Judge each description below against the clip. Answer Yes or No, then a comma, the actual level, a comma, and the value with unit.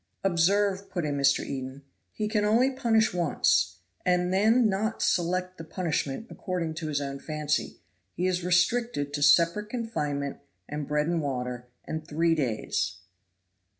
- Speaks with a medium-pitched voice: Yes, medium, 170 Hz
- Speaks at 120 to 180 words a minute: Yes, average, 150 wpm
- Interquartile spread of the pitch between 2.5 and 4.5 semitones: No, wide, 5.4 semitones